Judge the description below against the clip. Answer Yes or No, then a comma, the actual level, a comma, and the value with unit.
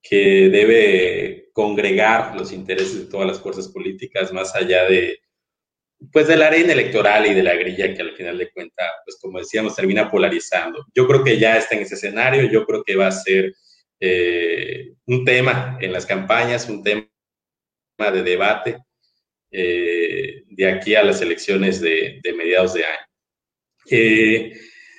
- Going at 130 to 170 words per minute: Yes, average, 165 wpm